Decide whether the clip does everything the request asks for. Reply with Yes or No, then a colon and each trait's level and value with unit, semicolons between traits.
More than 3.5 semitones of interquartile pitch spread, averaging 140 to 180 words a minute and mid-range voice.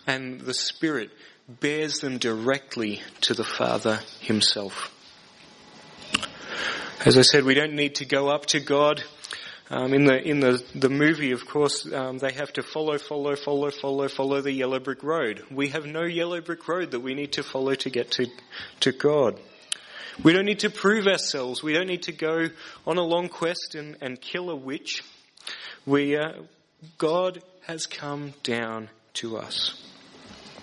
No: average, 3.2 semitones; average, 170 wpm; medium, 145 Hz